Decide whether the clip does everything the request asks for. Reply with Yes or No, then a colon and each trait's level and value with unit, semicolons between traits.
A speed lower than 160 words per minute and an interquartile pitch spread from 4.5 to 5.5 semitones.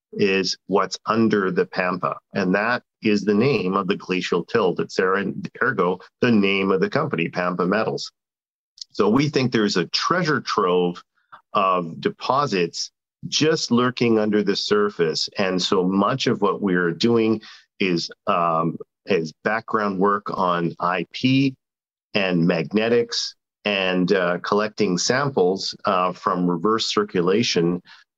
No: slow, 135 wpm; average, 3.8 semitones